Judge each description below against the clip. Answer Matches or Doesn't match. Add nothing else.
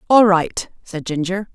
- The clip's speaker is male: Doesn't match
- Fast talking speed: Doesn't match